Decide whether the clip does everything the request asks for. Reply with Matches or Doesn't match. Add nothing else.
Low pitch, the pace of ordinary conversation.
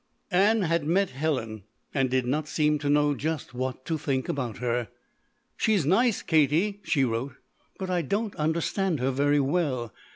Doesn't match